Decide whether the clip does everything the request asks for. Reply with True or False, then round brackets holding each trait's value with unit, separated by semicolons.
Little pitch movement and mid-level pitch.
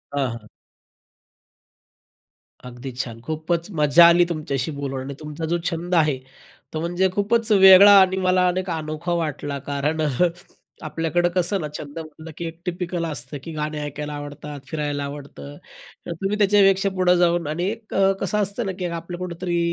False (3.7 semitones; 165 Hz)